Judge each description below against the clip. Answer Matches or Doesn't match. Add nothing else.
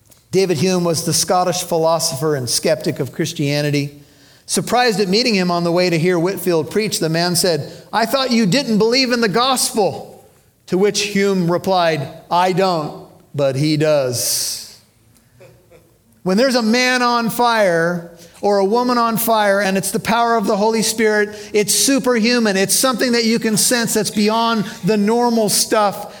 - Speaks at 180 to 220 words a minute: Doesn't match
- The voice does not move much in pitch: Doesn't match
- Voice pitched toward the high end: Matches